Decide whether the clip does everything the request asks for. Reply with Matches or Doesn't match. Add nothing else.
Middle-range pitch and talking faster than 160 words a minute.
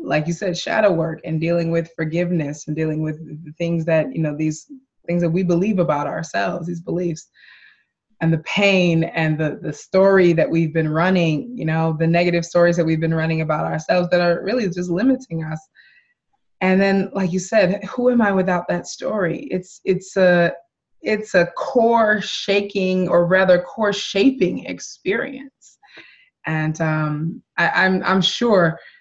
Matches